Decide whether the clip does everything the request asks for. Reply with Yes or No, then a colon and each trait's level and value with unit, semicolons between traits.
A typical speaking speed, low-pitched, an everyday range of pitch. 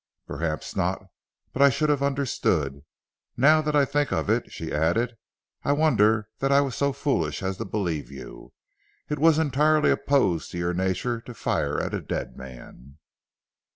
No: average, 170 wpm; low, 120 Hz; wide, 8.6 semitones